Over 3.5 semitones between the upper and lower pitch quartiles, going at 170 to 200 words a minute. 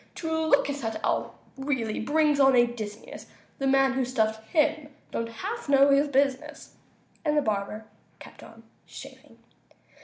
No: average, 4.3 semitones; average, 155 wpm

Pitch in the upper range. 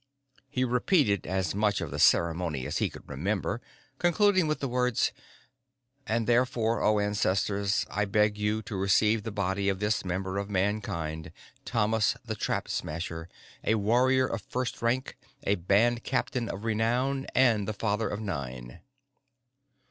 No: low, 105 Hz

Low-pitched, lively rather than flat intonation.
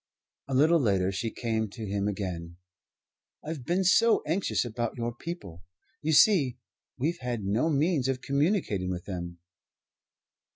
Yes: low, 120 Hz; wide, 7.9 semitones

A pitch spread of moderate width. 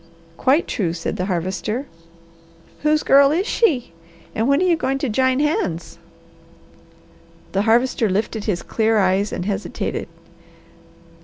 No: wide, 6.3 semitones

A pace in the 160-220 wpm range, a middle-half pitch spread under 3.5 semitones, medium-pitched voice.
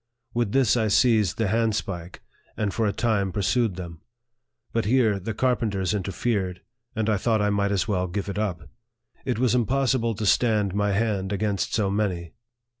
No: average, 180 wpm; average, 2.7 semitones; low, 105 Hz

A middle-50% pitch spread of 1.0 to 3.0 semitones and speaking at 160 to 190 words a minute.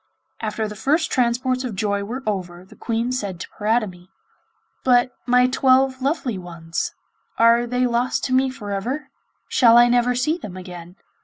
No: average, 4.2 semitones; average, 165 wpm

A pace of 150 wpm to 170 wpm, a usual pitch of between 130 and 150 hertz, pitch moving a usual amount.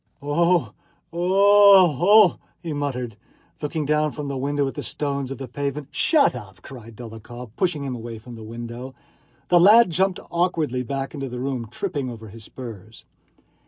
No: average, 165 wpm; medium, 140 Hz; wide, 5.9 semitones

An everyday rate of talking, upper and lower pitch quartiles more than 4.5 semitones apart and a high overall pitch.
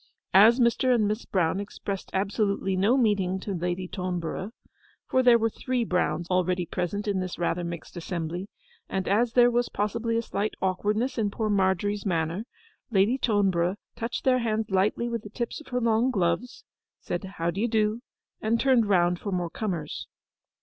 No: average, 170 wpm; average, 4.1 semitones; high, 205 Hz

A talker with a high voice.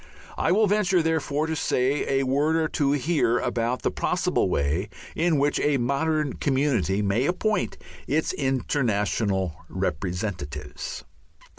No: low, 135 Hz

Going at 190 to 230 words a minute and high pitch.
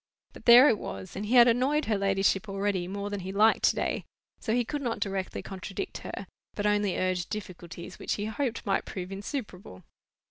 Yes: average, 200 wpm; high, 205 Hz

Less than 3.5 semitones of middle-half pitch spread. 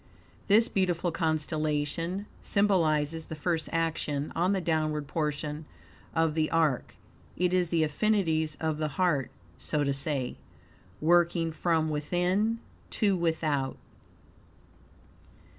Yes: narrow, 2.6 semitones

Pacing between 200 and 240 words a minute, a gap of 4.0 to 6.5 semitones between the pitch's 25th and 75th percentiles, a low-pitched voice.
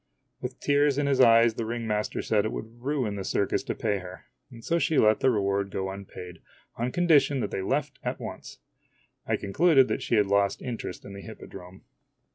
Yes: fast, 205 wpm; average, 5.1 semitones; low, 115 Hz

